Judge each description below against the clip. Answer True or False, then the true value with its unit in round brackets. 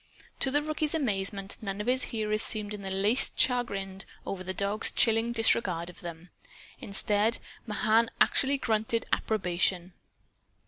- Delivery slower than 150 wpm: True (140 wpm)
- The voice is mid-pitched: False (210 Hz)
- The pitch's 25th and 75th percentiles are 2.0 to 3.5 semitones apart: True (3.2 semitones)